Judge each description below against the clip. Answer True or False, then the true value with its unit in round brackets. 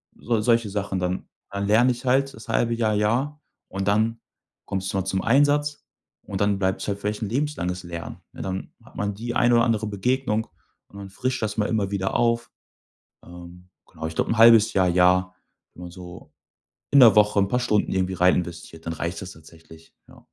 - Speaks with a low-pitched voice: True (100 Hz)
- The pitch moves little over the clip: False (4.0 semitones)